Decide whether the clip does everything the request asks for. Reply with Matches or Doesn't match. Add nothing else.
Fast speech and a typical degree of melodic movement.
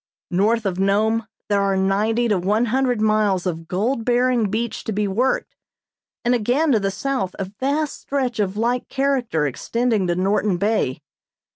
Doesn't match